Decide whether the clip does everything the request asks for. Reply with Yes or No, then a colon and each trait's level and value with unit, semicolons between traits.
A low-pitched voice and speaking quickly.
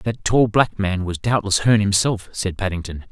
No: low, 100 Hz; average, 195 wpm